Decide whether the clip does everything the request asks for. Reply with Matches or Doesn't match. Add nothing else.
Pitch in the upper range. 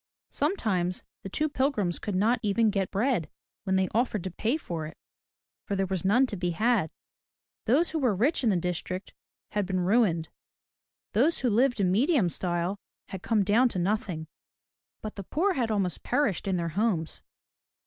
Matches